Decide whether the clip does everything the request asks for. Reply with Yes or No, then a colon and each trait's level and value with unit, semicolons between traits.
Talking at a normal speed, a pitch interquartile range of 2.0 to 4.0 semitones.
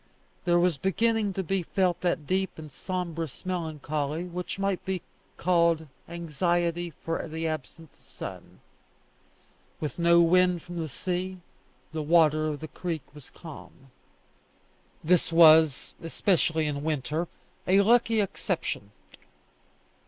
No: slow, 125 wpm; narrow, 2.6 semitones